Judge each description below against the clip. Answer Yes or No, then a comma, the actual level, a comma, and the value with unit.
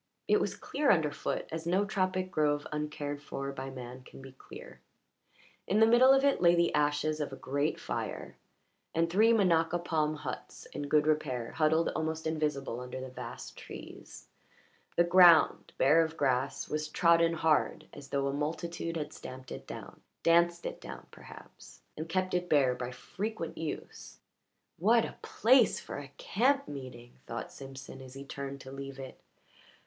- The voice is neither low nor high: Yes, medium, 155 Hz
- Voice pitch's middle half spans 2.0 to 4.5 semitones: Yes, average, 3.9 semitones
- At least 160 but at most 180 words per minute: Yes, average, 170 wpm